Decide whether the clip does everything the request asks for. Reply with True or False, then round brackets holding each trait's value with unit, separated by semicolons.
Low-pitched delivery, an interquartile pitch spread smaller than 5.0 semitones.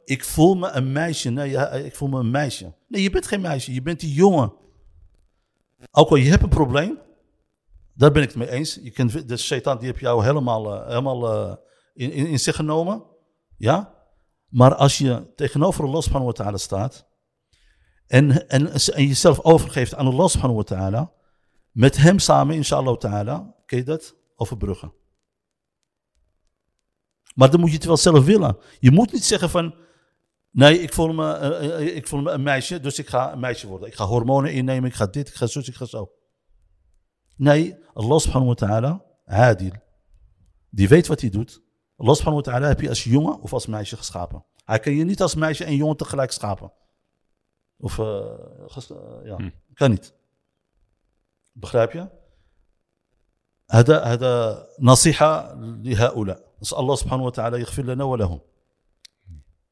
False (130 Hz; 5.4 semitones)